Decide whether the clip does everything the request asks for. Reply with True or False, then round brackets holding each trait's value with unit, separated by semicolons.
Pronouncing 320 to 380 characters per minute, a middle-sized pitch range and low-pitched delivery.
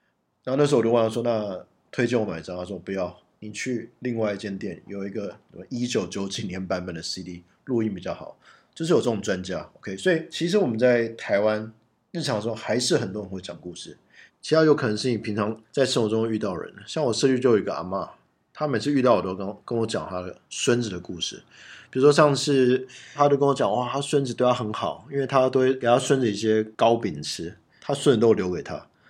True (335 characters per minute; 4.1 semitones; 115 Hz)